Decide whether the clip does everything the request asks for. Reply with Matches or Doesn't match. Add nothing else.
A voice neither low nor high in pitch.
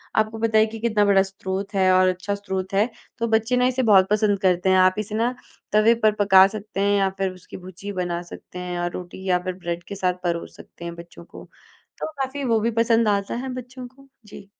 Doesn't match